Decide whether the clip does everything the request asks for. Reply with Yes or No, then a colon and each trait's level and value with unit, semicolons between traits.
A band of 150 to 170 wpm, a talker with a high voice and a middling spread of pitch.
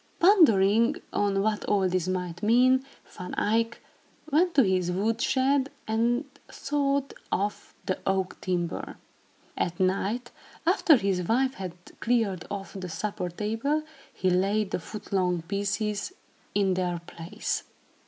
No: slow, 135 wpm; high, 205 Hz; average, 4.6 semitones